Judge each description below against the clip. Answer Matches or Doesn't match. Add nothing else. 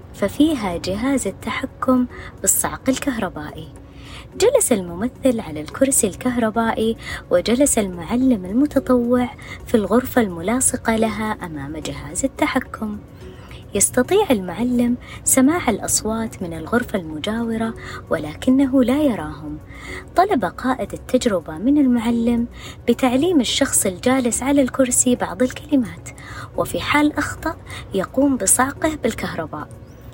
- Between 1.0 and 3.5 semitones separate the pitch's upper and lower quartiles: Doesn't match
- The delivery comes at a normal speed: Matches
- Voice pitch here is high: Matches